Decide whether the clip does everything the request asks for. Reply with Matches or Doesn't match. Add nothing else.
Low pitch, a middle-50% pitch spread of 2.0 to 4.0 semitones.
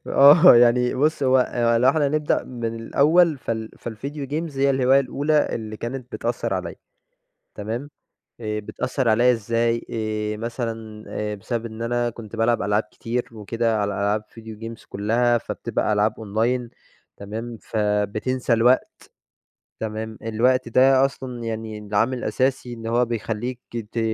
Matches